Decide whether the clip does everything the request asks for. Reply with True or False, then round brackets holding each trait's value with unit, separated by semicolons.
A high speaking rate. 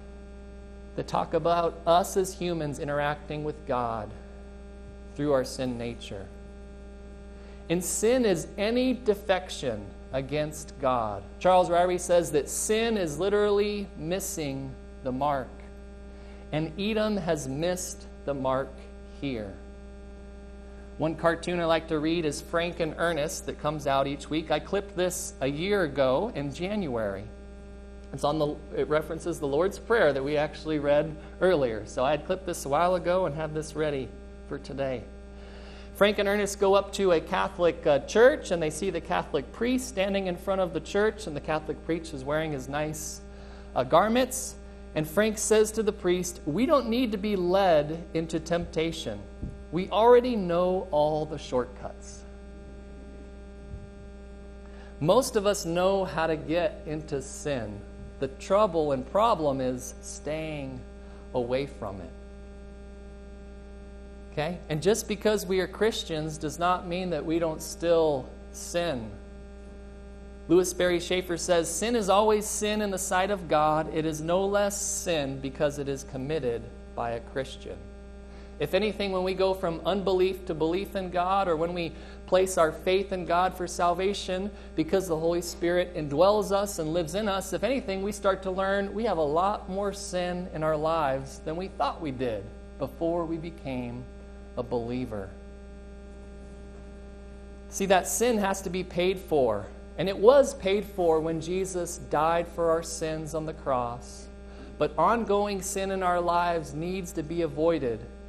False (160 wpm)